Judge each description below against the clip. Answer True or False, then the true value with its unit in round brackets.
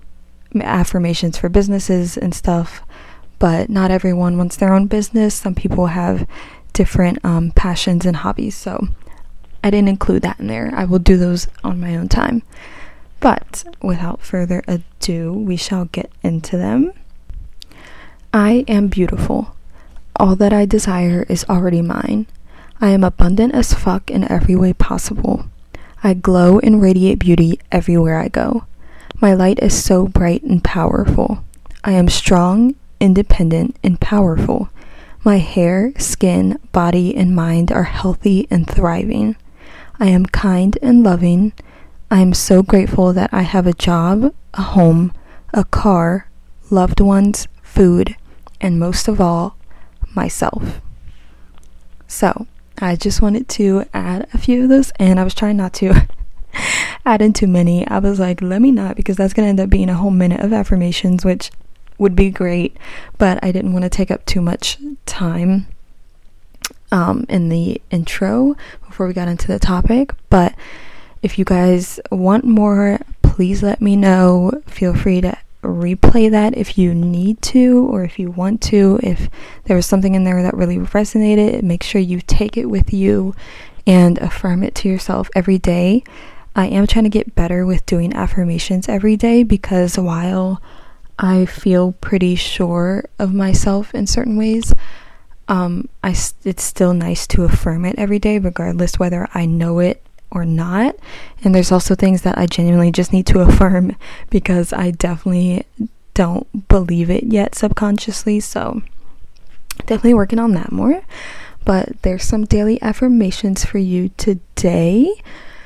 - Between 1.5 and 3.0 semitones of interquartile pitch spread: True (2.6 semitones)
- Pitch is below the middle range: False (190 Hz)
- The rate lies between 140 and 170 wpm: True (155 wpm)